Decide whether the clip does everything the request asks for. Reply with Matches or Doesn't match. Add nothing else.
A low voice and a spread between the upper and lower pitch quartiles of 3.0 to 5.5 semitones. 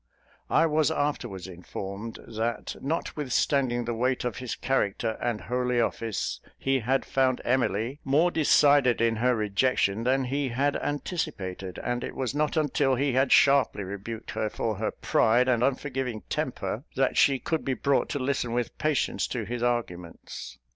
Matches